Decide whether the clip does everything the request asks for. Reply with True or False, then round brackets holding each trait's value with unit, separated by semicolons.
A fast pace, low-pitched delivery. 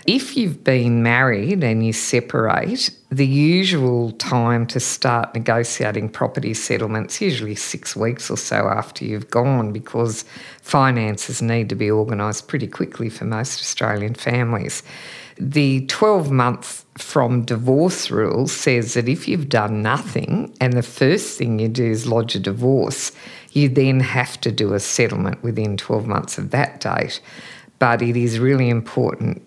False (155 wpm; 120 Hz)